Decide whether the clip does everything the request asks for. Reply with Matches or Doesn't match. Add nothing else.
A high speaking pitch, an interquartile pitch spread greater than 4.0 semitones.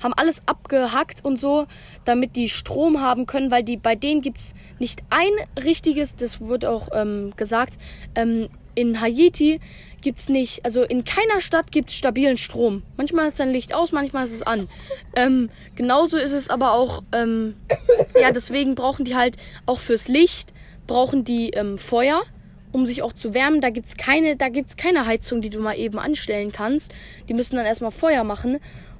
Doesn't match